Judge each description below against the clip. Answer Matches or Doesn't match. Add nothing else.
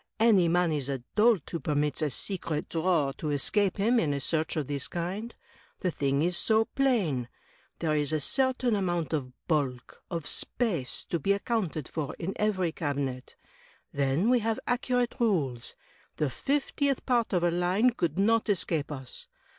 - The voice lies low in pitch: Doesn't match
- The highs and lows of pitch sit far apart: Matches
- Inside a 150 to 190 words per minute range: Matches